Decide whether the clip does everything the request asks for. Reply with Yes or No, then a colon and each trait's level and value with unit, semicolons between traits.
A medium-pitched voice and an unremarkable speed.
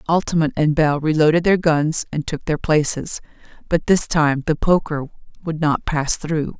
Yes: medium, 155 Hz; average, 175 wpm